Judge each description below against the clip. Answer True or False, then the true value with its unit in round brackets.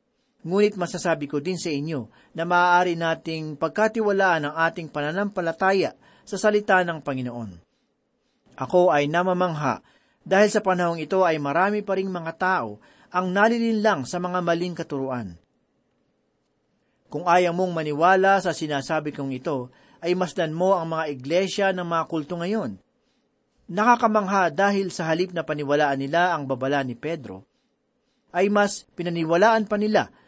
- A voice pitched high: False (175 Hz)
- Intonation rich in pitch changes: False (3.9 semitones)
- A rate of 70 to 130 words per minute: False (140 wpm)